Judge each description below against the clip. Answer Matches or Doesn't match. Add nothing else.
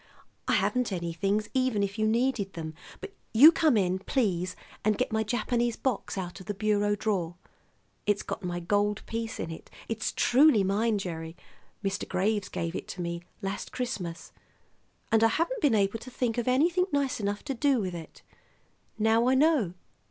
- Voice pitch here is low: Doesn't match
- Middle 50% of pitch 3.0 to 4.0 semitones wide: Doesn't match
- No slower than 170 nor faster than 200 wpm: Matches